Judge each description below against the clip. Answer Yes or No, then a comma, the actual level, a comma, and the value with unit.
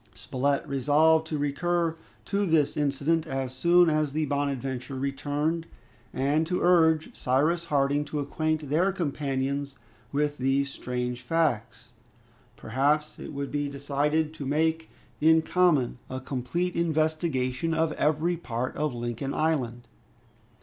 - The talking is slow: Yes, slow, 130 wpm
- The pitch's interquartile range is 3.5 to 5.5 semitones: No, average, 3.0 semitones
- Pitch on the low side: No, medium, 145 Hz